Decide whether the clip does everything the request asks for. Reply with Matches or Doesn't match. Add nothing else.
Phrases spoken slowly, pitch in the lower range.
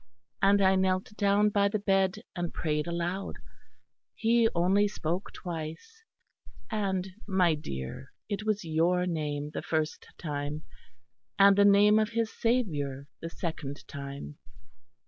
Doesn't match